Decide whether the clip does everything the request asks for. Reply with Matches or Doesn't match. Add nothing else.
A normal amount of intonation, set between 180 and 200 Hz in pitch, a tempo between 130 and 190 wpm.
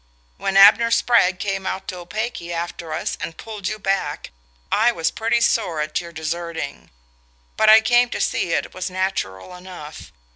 Matches